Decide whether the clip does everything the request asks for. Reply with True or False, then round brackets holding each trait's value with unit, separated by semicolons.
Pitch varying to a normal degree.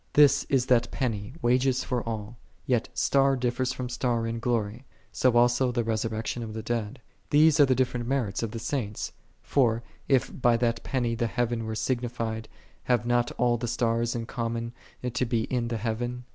False (1.6 semitones)